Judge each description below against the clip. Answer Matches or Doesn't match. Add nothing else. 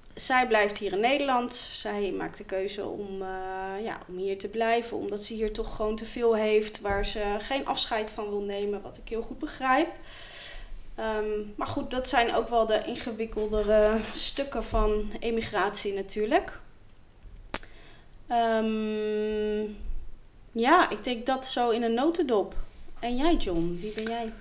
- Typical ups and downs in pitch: Doesn't match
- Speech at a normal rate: Matches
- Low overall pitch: Doesn't match